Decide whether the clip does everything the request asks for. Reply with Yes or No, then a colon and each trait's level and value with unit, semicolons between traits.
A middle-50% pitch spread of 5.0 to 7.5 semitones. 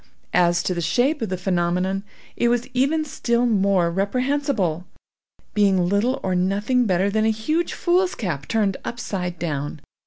Yes: wide, 5.5 semitones